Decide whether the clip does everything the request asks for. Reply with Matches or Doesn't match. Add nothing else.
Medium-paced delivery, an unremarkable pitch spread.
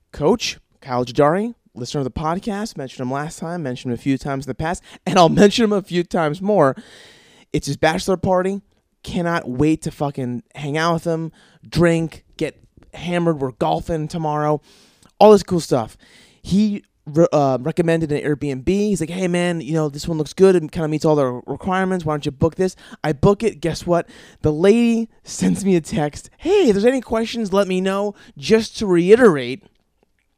Matches